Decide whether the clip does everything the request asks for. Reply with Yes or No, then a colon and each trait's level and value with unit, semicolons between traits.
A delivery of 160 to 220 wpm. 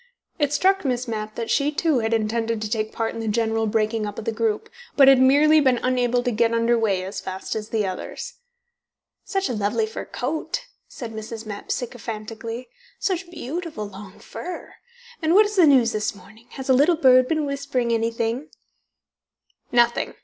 Yes: average, 180 wpm